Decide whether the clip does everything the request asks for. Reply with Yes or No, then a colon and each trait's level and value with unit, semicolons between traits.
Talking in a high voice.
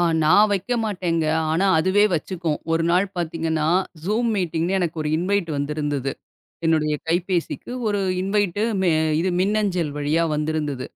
No: medium, 170 Hz